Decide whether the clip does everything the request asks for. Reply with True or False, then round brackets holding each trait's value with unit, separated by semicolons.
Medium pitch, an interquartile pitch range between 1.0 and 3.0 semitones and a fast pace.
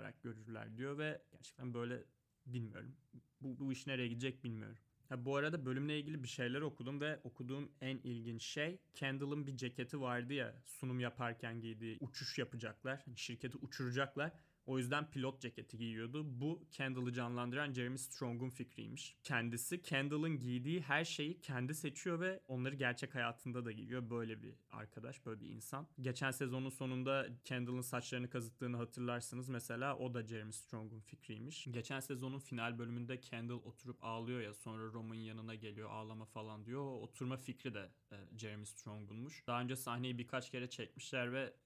False (125 Hz; 2.5 semitones; 155 wpm)